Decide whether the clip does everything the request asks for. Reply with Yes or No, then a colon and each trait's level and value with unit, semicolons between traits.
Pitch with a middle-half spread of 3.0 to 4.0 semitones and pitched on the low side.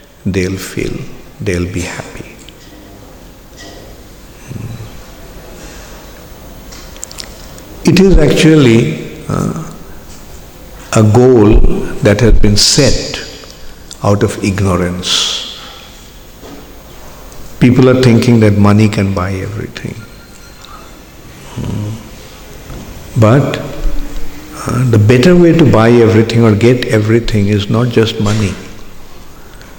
Yes: average, 3.5 semitones; low, 110 Hz